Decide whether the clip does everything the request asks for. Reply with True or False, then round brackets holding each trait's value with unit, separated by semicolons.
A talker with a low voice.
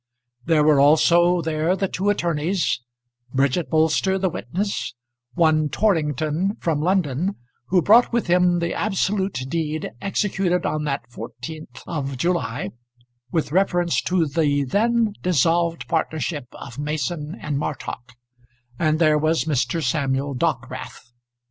False (160 Hz)